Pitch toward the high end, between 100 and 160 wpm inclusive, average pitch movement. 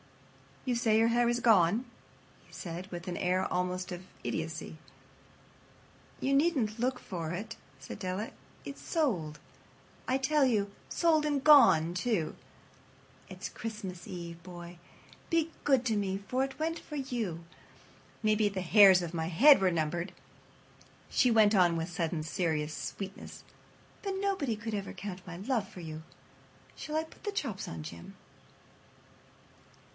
No: high, 200 Hz; average, 145 wpm; wide, 6.5 semitones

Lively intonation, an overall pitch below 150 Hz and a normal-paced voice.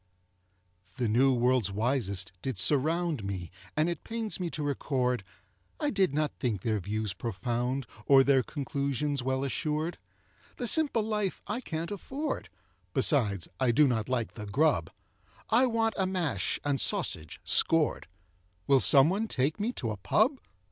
Yes: wide, 6.7 semitones; medium, 140 Hz; average, 150 wpm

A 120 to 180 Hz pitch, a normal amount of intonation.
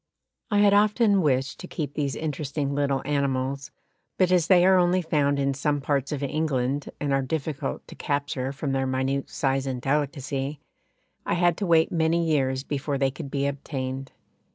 Yes: medium, 140 Hz; average, 3.0 semitones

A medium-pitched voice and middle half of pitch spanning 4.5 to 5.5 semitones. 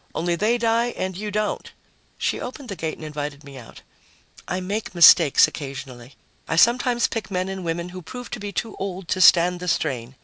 Yes: medium, 180 Hz; average, 5.2 semitones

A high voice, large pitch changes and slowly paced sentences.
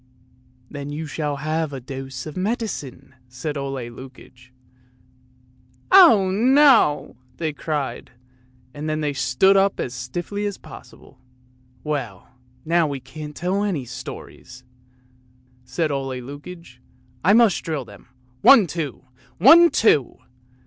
No: medium, 150 Hz; wide, 5.9 semitones; slow, 130 wpm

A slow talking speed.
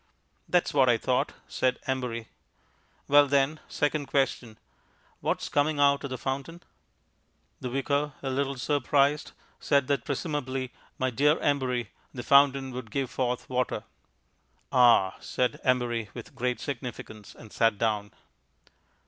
Yes: slow, 130 wpm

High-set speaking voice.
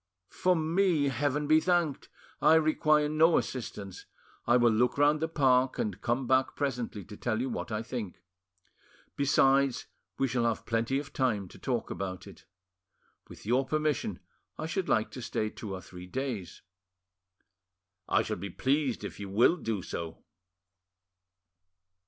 No: low, 130 Hz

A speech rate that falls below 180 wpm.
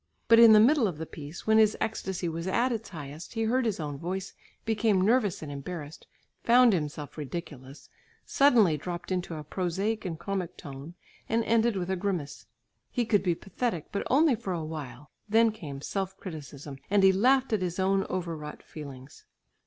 No: average, 185 wpm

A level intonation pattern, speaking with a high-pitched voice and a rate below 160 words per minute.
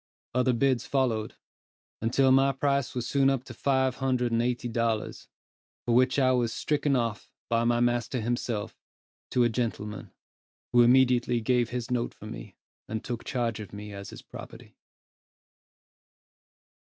No: narrow, 2.0 semitones; low, 120 Hz; average, 150 wpm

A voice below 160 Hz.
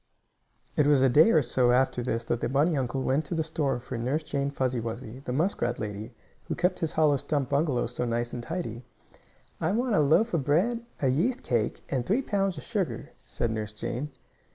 Yes: medium, 140 Hz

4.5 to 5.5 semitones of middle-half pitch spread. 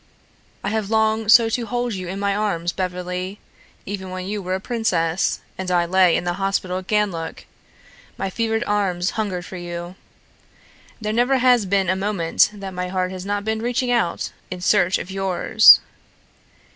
No: average, 3.0 semitones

